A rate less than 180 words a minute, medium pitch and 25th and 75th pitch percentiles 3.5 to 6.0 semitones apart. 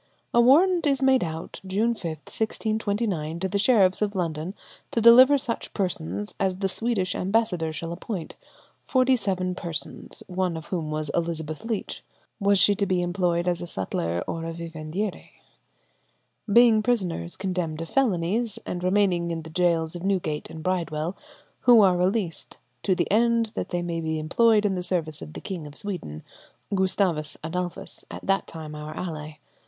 Yes: average, 170 wpm; medium, 180 Hz; average, 4.3 semitones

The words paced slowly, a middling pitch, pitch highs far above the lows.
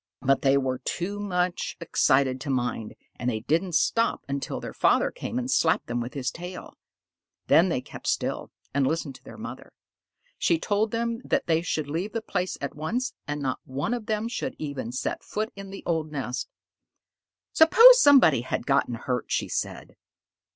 No: average, 185 wpm; medium, 160 Hz; wide, 7.6 semitones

